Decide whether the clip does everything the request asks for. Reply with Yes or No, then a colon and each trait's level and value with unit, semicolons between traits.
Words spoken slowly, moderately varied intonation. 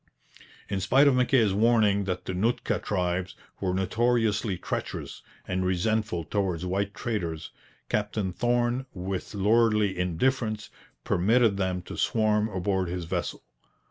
Yes: slow, 125 wpm; average, 3.5 semitones